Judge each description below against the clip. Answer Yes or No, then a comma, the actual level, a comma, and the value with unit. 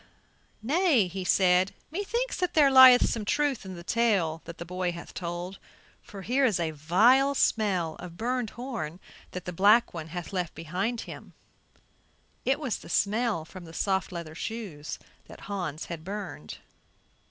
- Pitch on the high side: Yes, high, 195 Hz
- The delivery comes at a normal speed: Yes, average, 165 wpm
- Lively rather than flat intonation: Yes, wide, 5.8 semitones